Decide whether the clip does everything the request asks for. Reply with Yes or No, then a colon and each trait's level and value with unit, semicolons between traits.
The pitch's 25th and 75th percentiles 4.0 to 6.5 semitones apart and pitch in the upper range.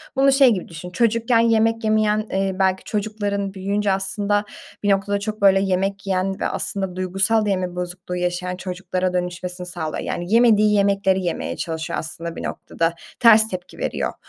No: narrow, 2.6 semitones; high, 195 Hz